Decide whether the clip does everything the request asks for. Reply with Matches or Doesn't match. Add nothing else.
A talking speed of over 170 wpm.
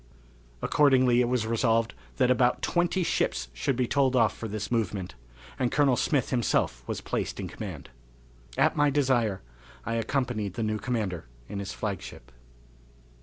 Doesn't match